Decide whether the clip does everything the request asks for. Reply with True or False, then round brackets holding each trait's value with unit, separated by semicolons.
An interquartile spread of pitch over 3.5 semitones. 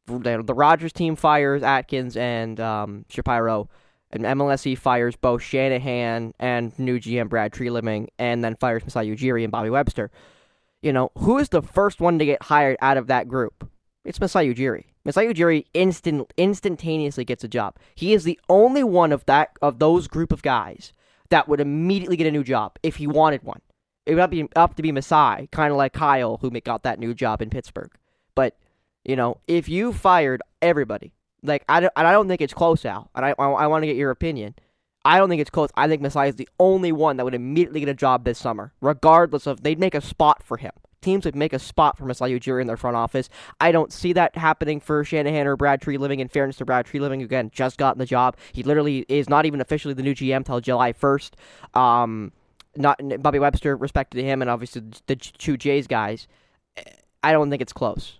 True (3.9 semitones)